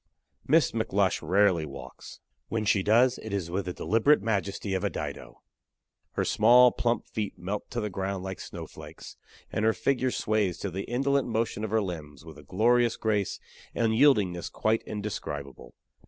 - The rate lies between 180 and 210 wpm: No, average, 170 wpm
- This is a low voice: Yes, low, 105 Hz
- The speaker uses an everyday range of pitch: Yes, average, 3.5 semitones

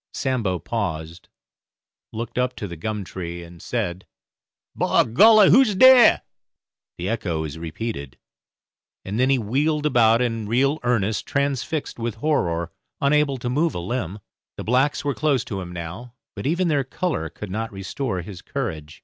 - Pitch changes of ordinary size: No, wide, 7.5 semitones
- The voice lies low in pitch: Yes, low, 115 Hz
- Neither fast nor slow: Yes, average, 160 wpm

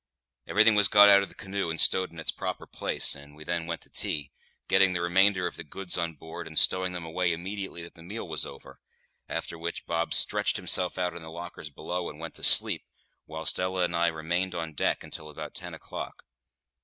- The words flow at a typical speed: No, fast, 220 wpm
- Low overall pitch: Yes, very low, 85 Hz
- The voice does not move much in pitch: Yes, narrow, 2.3 semitones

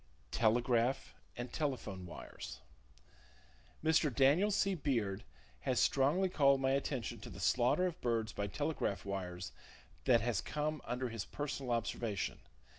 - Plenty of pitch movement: No, average, 4.7 semitones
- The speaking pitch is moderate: No, low, 125 Hz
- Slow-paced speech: Yes, slow, 130 wpm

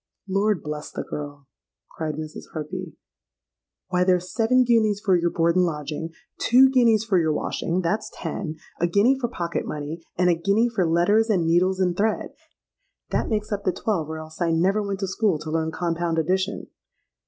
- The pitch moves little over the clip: No, average, 4.2 semitones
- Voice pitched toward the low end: No, medium, 180 Hz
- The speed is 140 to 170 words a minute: No, average, 185 wpm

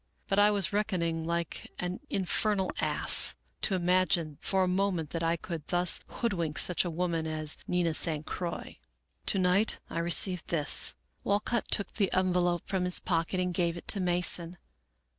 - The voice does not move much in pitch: Yes, narrow, 2.1 semitones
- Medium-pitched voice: Yes, medium, 180 Hz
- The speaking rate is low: No, average, 180 wpm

